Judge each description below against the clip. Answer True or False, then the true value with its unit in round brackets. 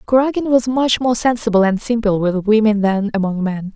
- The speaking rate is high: False (190 wpm)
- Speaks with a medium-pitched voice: False (220 Hz)